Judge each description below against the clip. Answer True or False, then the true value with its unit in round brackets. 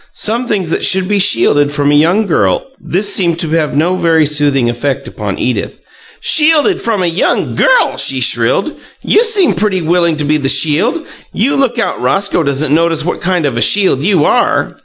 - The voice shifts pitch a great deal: True (5.8 semitones)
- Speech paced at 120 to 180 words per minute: False (200 wpm)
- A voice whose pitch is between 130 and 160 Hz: False (170 Hz)